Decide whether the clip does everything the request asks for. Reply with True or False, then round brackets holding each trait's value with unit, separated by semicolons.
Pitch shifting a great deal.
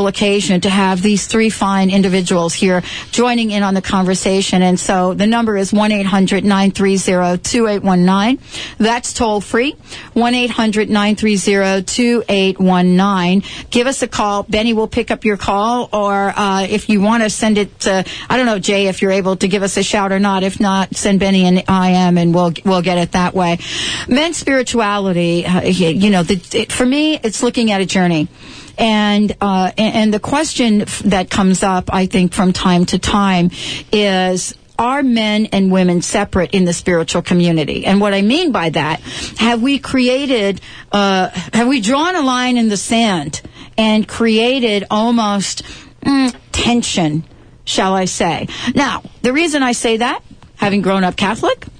False (3.3 semitones)